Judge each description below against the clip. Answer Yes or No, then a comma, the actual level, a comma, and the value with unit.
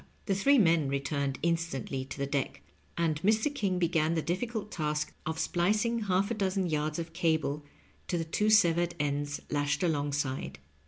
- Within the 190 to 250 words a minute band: No, average, 165 wpm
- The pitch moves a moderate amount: Yes, average, 4.7 semitones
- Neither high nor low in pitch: Yes, medium, 165 Hz